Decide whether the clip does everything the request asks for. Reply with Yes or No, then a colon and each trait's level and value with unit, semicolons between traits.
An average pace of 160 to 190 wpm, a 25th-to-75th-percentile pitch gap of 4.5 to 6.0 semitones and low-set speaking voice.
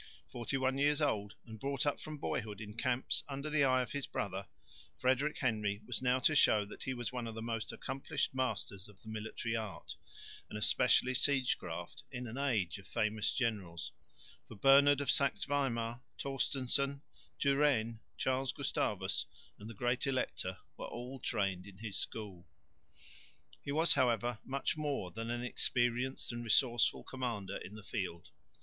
No: average, 165 wpm; average, 4.0 semitones; low, 120 Hz